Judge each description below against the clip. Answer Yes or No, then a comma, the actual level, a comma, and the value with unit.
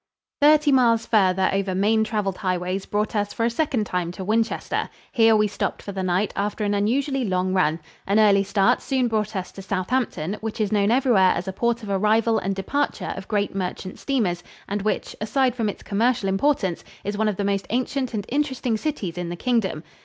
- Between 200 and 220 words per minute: Yes, fast, 205 wpm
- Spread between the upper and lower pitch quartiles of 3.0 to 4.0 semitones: Yes, average, 3.4 semitones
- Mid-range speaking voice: No, high, 210 Hz